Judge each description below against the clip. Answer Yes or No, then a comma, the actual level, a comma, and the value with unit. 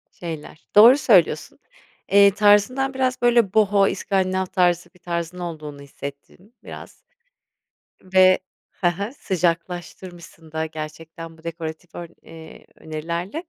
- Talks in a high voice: No, medium, 175 Hz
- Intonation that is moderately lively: Yes, average, 3.6 semitones